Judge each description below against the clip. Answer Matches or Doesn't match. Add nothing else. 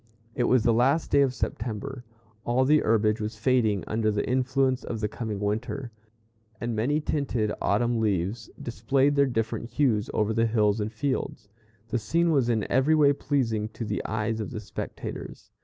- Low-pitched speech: Matches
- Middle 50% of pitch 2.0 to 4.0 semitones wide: Matches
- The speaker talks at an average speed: Matches